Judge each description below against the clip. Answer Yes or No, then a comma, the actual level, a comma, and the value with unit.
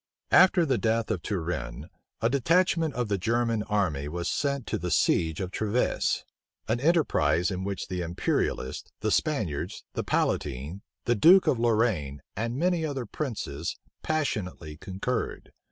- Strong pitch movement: Yes, wide, 7.6 semitones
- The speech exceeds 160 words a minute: No, average, 145 wpm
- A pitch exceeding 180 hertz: No, low, 110 Hz